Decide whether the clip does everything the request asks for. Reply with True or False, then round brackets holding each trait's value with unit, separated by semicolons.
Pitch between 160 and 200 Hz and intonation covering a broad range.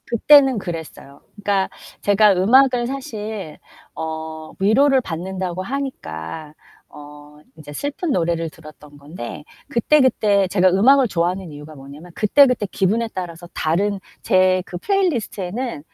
True (190 Hz; 6.7 semitones)